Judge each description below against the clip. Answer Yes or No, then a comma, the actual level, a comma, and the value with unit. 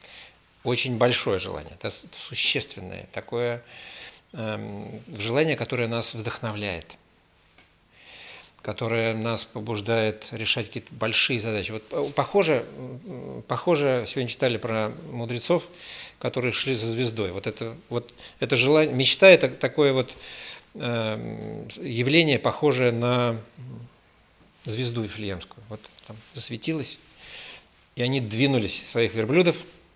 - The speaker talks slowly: Yes, slow, 100 wpm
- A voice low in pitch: Yes, low, 120 Hz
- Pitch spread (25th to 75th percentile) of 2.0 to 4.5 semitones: Yes, average, 2.9 semitones